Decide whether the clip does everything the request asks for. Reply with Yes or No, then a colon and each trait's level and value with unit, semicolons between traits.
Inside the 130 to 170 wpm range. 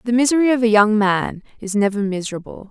No: average, 200 wpm